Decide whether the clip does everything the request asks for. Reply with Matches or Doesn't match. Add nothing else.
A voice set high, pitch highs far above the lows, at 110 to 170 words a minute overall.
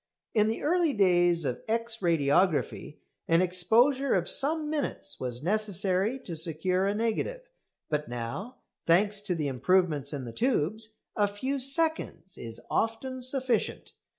Matches